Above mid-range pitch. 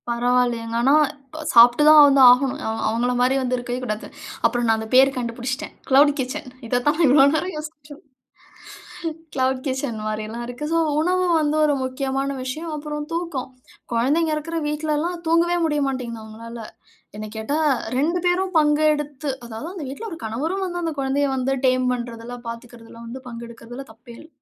Yes: very high, 265 Hz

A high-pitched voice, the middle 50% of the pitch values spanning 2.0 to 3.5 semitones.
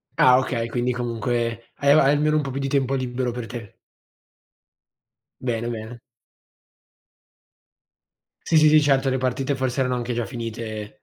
No: low, 125 Hz; narrow, 2.5 semitones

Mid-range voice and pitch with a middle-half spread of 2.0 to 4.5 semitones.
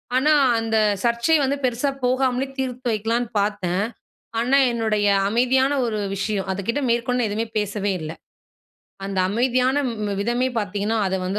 No: high, 230 Hz; average, 3.6 semitones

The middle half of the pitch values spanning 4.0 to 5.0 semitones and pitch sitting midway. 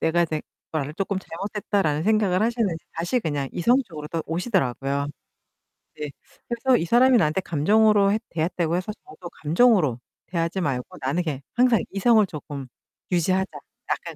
No: wide, 5.6 semitones; medium, 175 Hz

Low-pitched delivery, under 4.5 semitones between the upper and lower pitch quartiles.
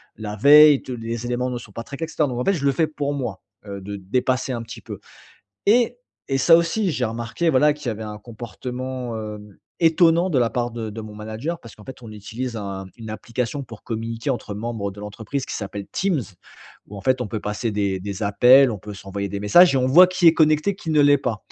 No: low, 120 Hz; average, 5.2 semitones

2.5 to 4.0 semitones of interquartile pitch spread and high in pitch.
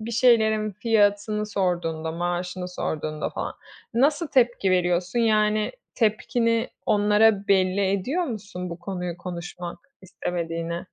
Yes: average, 3.7 semitones; high, 200 Hz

